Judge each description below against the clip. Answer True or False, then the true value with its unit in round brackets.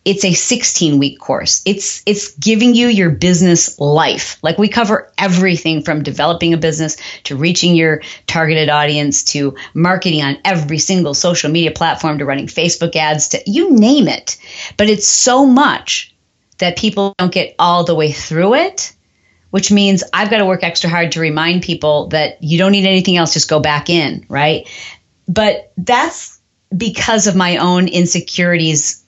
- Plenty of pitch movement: False (3.9 semitones)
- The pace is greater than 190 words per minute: False (170 wpm)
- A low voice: False (175 Hz)